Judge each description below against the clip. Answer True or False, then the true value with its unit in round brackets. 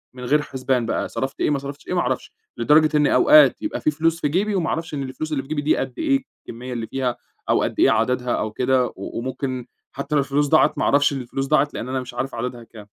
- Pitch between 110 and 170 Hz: True (135 Hz)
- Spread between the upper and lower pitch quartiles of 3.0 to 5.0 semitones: True (3.3 semitones)